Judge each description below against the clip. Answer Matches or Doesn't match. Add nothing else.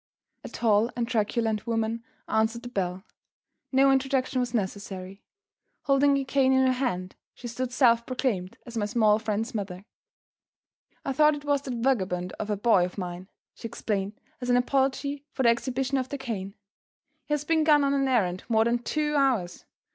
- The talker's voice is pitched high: Matches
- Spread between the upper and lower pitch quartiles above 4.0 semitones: Matches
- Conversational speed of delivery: Matches